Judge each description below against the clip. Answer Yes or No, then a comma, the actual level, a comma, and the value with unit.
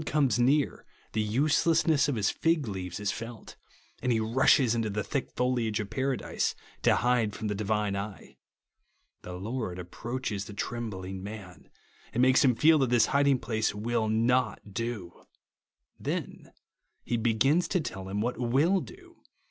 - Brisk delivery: No, average, 160 wpm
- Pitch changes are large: No, average, 4.0 semitones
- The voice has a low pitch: Yes, low, 115 Hz